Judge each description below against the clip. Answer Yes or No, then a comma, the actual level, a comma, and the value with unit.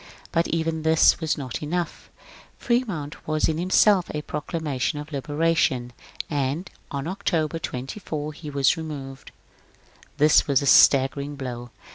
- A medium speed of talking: No, slow, 130 wpm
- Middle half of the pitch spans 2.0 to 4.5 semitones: Yes, average, 2.8 semitones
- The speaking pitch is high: No, medium, 150 Hz